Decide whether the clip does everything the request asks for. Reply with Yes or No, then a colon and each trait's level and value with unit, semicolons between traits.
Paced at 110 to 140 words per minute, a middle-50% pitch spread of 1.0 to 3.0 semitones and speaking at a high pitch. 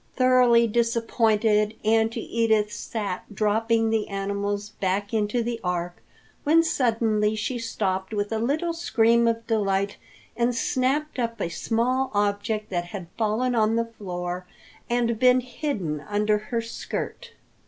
Yes: slow, 135 wpm; narrow, 2.4 semitones; high, 225 Hz